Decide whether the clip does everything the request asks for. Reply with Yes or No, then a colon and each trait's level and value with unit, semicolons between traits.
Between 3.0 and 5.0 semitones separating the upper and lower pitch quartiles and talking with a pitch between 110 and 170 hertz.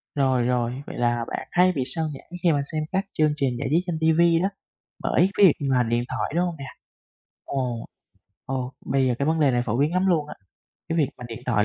Yes: average, 4.7 semitones; medium, 140 Hz